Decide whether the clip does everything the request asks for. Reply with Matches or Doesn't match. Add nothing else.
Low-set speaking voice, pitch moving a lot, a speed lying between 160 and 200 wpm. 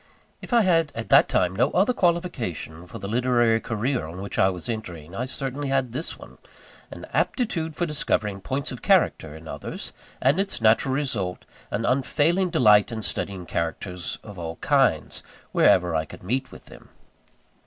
Matches